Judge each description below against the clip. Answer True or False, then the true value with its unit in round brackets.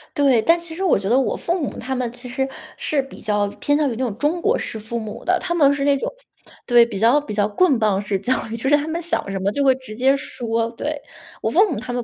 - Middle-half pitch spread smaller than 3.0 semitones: False (4.8 semitones)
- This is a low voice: False (260 Hz)